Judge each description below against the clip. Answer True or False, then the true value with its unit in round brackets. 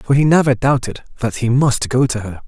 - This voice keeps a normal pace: False (245 wpm)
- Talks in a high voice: False (125 Hz)